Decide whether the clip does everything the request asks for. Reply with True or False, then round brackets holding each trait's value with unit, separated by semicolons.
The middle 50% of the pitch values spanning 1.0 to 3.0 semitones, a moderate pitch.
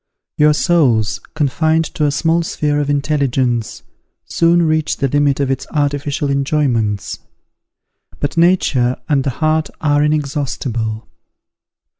True (2.7 semitones; 145 Hz)